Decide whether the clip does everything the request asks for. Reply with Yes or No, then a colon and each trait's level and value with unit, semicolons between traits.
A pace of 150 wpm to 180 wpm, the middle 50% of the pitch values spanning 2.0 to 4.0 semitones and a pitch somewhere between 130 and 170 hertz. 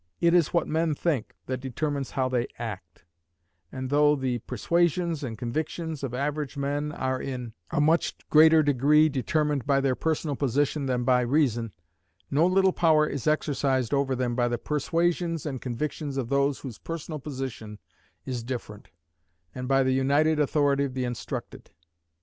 Yes: average, 160 wpm; average, 3.1 semitones; medium, 140 Hz